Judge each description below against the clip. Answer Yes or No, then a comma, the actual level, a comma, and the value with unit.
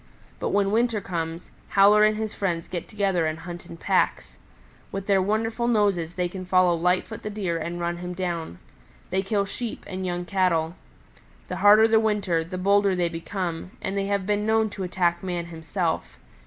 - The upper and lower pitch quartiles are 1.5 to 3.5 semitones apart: Yes, average, 2.9 semitones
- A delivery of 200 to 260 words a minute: No, average, 185 wpm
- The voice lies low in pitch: No, medium, 185 Hz